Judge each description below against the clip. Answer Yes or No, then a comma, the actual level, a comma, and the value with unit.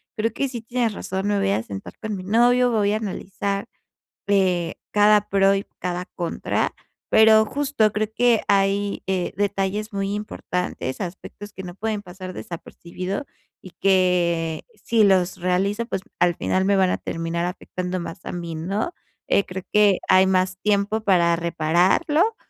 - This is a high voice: Yes, high, 195 Hz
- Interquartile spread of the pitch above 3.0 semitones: No, average, 2.7 semitones